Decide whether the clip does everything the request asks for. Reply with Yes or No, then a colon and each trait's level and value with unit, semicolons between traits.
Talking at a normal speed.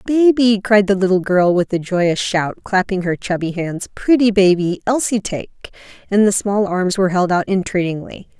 Yes: average, 180 wpm